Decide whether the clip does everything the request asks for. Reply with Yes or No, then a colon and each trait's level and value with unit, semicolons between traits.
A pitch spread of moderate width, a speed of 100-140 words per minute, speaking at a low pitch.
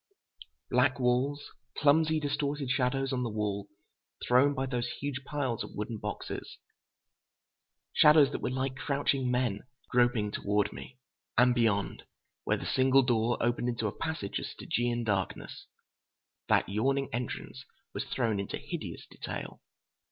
Yes: average, 3.0 semitones; slow, 135 wpm; low, 125 Hz